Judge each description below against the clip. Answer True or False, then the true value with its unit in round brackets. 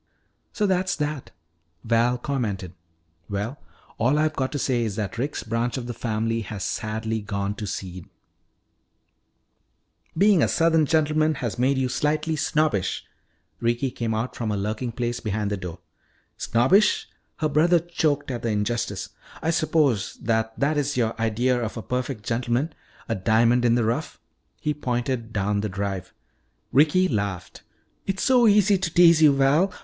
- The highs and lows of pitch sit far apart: True (5.7 semitones)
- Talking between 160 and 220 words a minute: True (165 wpm)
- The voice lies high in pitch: False (120 Hz)